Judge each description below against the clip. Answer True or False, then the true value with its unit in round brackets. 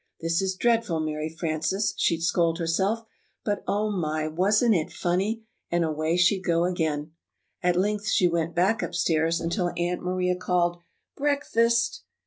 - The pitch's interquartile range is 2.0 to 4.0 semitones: True (3.7 semitones)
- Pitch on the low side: False (180 Hz)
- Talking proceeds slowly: False (145 wpm)